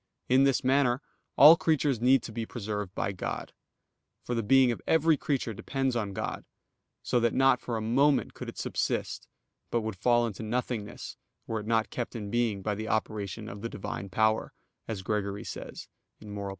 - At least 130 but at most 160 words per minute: No, average, 185 wpm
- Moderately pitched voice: No, low, 115 Hz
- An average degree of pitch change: Yes, average, 3.4 semitones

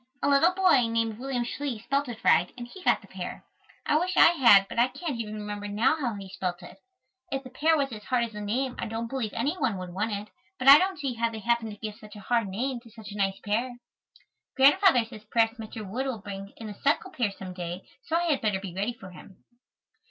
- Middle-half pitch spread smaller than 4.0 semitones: No, average, 4.5 semitones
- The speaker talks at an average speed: No, fast, 250 wpm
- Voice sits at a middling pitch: No, high, 230 Hz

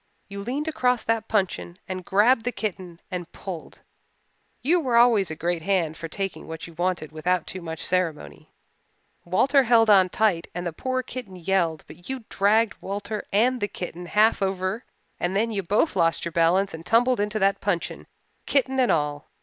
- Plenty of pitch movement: No, average, 4.6 semitones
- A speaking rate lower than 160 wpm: No, average, 180 wpm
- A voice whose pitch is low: No, high, 195 Hz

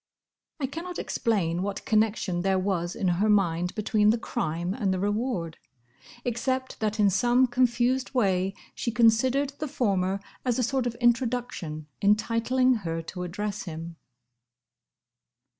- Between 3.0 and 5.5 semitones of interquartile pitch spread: Yes, average, 4.9 semitones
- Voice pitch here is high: Yes, high, 215 Hz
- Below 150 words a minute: Yes, average, 140 wpm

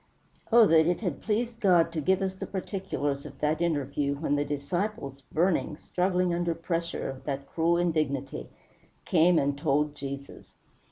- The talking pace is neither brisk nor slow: Yes, average, 160 wpm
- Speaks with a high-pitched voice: No, medium, 165 Hz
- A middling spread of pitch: Yes, average, 4.2 semitones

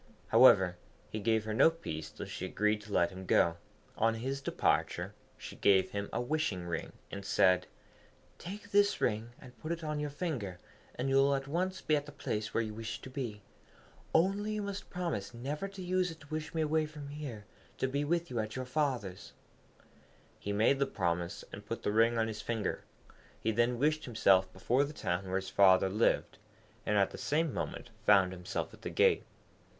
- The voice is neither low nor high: No, low, 120 Hz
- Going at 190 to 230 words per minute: Yes, average, 200 wpm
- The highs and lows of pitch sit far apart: Yes, wide, 7.0 semitones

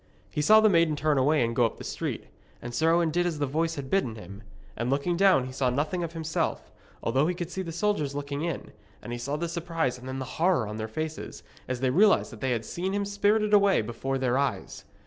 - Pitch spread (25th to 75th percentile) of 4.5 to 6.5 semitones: Yes, average, 5.2 semitones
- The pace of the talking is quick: Yes, fast, 245 wpm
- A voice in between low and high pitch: Yes, medium, 150 Hz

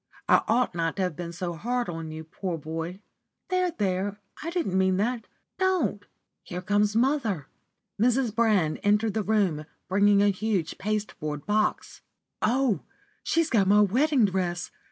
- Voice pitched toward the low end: No, high, 205 Hz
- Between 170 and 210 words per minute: No, average, 155 wpm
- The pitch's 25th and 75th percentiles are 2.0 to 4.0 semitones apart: No, average, 4.4 semitones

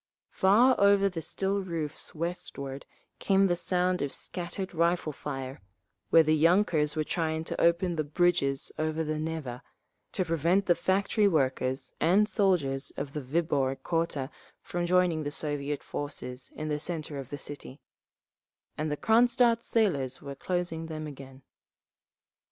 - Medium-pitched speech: Yes, medium, 160 Hz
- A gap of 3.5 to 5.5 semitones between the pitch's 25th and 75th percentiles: Yes, average, 3.9 semitones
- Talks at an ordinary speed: Yes, average, 145 wpm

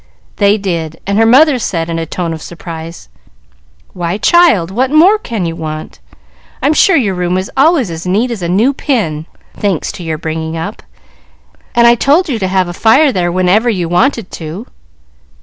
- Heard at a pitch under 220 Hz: Yes, high, 190 Hz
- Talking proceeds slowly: No, average, 185 wpm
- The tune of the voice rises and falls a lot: Yes, wide, 6.3 semitones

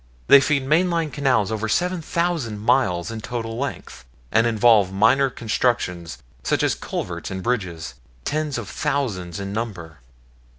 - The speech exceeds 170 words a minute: No, average, 145 wpm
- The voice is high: No, low, 115 Hz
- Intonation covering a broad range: Yes, wide, 5.9 semitones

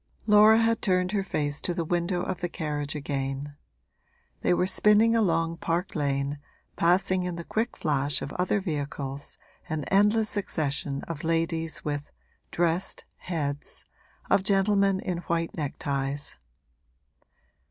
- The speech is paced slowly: Yes, slow, 130 wpm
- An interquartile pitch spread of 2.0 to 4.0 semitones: No, average, 4.7 semitones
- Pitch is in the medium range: Yes, medium, 170 Hz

